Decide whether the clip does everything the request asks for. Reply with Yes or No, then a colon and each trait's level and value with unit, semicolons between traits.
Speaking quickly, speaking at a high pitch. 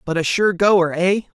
No: fast, 215 wpm; medium, 180 Hz